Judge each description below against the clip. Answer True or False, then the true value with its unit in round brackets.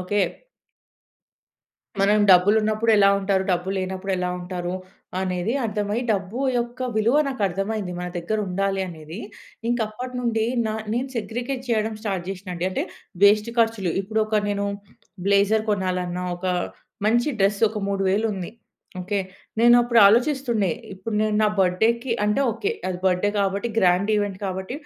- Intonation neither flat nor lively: True (3.0 semitones)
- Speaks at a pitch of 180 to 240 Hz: True (205 Hz)